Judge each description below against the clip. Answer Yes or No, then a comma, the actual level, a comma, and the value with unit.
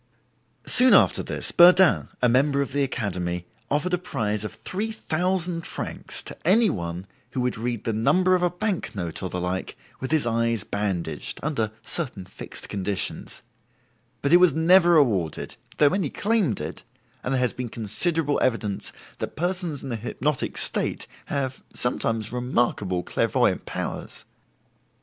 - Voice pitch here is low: Yes, low, 130 Hz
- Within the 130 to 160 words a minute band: Yes, average, 155 wpm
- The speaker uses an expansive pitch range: Yes, wide, 8.4 semitones